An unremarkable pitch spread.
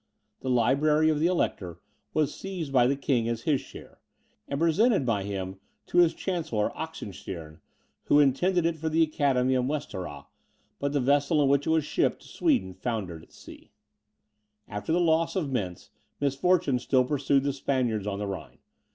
No: wide, 5.8 semitones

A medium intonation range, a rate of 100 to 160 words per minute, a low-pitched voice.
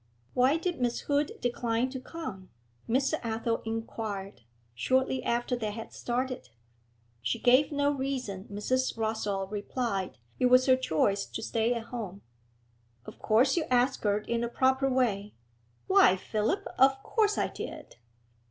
No: average, 3.7 semitones; average, 145 wpm; high, 240 Hz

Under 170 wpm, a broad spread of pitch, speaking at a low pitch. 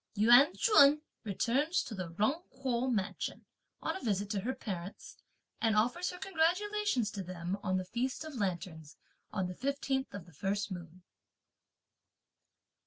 No: average, 150 wpm; wide, 6.9 semitones; high, 220 Hz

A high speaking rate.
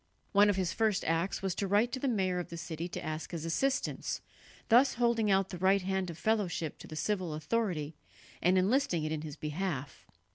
Yes: fast, 210 wpm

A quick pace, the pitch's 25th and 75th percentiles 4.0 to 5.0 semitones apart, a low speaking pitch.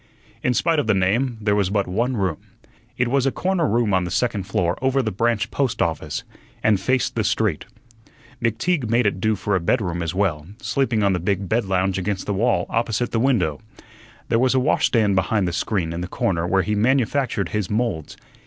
Yes: fast, 210 wpm; average, 4.6 semitones; low, 105 Hz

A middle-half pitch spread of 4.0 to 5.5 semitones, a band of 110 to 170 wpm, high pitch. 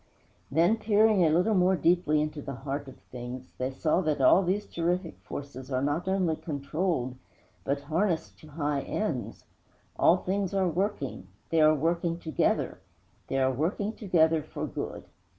No: average, 4.6 semitones; average, 165 wpm; medium, 160 Hz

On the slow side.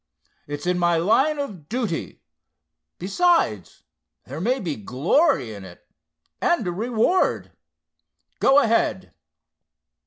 Yes: slow, 100 wpm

